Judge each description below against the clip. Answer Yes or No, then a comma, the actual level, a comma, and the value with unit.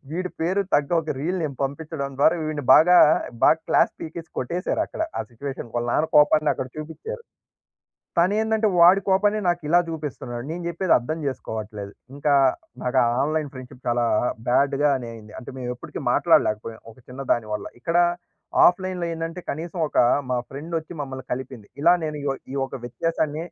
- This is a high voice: No, medium, 150 Hz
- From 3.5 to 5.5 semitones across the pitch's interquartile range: Yes, average, 4.8 semitones